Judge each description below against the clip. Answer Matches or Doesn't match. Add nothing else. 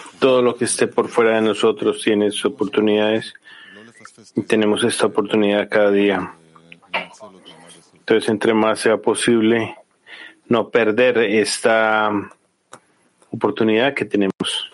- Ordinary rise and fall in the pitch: Doesn't match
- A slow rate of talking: Matches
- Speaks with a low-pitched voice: Matches